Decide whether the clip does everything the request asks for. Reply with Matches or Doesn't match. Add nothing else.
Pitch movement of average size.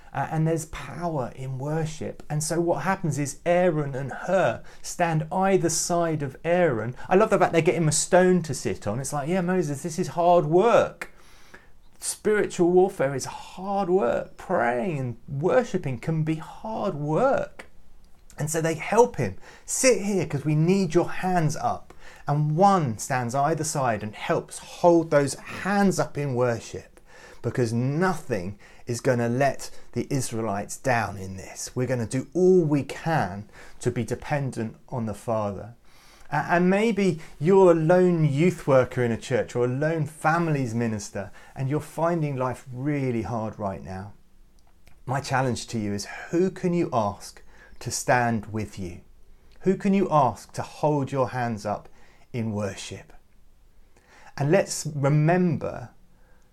Doesn't match